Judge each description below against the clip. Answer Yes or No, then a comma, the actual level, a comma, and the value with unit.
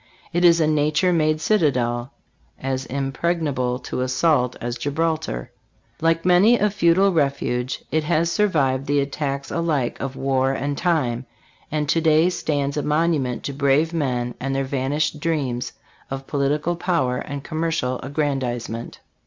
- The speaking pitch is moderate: Yes, medium, 145 Hz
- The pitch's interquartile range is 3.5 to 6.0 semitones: Yes, average, 3.8 semitones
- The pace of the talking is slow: No, average, 145 wpm